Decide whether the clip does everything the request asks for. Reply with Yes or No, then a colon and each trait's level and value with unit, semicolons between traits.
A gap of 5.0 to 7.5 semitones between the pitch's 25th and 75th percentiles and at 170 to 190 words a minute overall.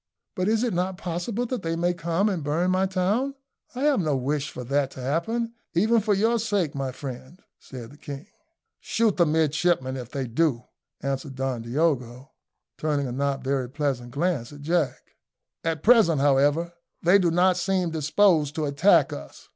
Yes: average, 5.3 semitones; average, 180 wpm